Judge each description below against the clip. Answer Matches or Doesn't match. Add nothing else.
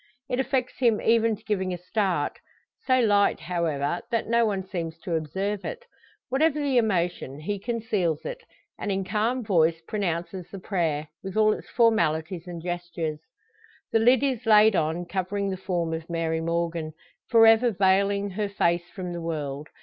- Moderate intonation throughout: Matches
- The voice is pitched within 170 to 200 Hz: Matches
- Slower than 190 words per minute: Matches